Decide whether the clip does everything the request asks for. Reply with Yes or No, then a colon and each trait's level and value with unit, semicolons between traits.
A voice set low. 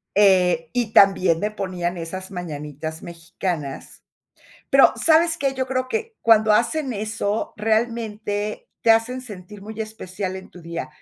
No: high, 205 Hz